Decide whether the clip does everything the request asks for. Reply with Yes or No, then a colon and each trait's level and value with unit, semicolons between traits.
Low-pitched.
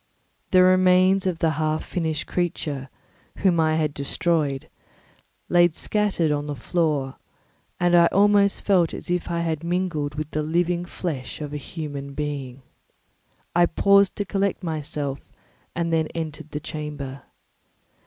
No: medium, 165 Hz